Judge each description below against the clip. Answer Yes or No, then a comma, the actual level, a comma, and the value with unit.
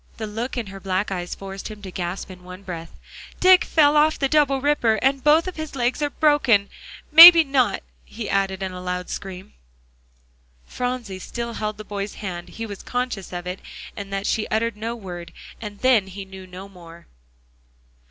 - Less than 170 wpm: No, average, 190 wpm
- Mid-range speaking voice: No, high, 210 Hz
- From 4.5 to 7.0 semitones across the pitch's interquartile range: Yes, average, 5.1 semitones